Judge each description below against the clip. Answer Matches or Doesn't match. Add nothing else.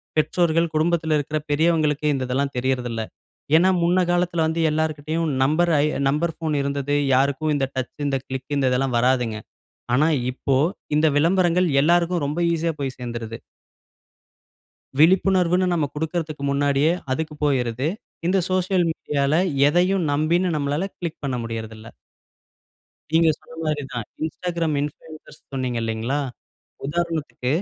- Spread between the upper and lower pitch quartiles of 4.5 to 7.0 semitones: Doesn't match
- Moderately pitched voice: Matches